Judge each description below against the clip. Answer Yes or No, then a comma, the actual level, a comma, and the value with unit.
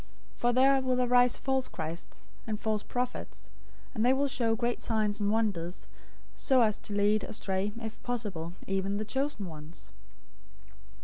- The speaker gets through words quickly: No, average, 160 wpm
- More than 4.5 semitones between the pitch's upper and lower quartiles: No, average, 3.8 semitones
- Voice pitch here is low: No, high, 220 Hz